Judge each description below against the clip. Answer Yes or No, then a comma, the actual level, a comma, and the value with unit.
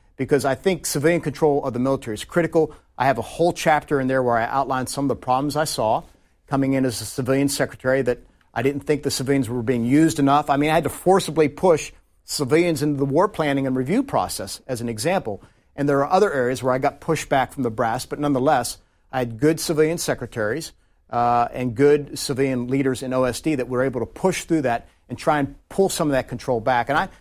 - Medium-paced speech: No, fast, 230 wpm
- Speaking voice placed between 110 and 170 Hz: Yes, medium, 140 Hz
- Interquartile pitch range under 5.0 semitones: Yes, average, 3.1 semitones